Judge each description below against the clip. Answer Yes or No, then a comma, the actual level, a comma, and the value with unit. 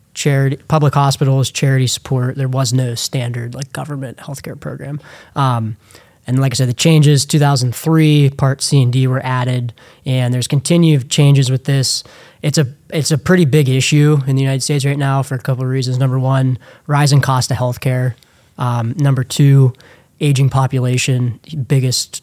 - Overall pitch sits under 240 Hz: Yes, low, 135 Hz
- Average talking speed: Yes, average, 175 wpm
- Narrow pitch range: Yes, narrow, 2.1 semitones